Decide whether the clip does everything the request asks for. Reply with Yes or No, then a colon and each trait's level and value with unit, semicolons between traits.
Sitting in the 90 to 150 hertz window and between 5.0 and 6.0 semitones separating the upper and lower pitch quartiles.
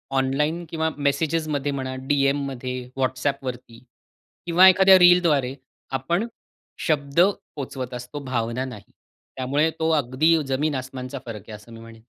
No: low, 135 Hz; average, 3.5 semitones